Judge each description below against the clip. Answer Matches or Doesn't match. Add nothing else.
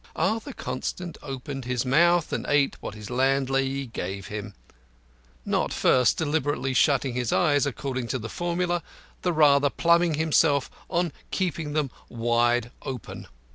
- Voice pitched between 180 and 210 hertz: Doesn't match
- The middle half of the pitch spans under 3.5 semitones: Doesn't match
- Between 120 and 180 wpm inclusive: Matches